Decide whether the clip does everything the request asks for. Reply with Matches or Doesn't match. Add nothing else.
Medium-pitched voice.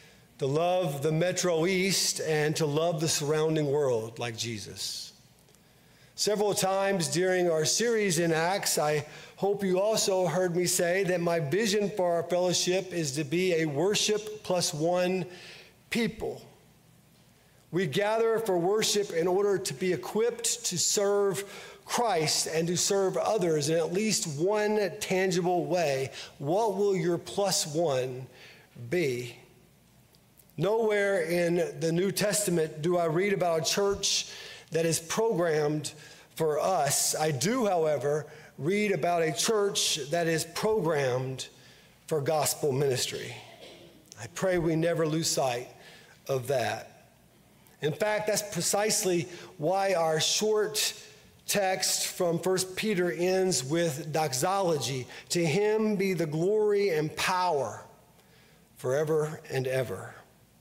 Matches